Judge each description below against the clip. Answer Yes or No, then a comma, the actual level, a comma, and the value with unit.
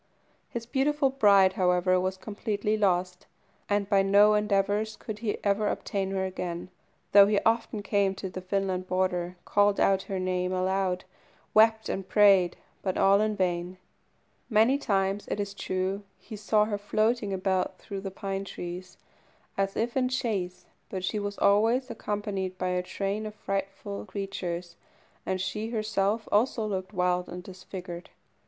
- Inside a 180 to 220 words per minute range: No, average, 155 wpm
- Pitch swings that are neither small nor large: No, narrow, 2.3 semitones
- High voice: Yes, high, 195 Hz